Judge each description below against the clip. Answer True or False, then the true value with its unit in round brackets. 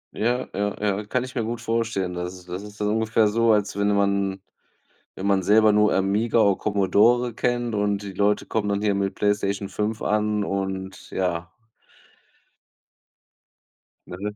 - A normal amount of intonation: False (1.9 semitones)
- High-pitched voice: False (105 Hz)